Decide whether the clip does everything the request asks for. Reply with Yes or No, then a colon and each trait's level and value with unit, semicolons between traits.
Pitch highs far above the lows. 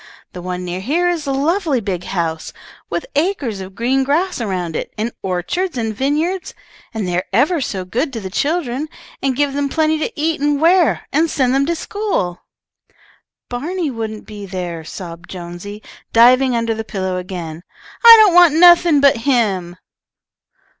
Yes: wide, 8.7 semitones